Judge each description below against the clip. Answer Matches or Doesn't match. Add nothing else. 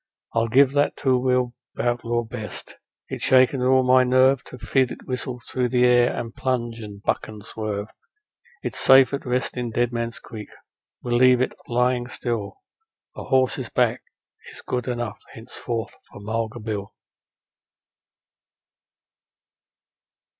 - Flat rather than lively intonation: Matches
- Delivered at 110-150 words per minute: Matches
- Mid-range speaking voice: Doesn't match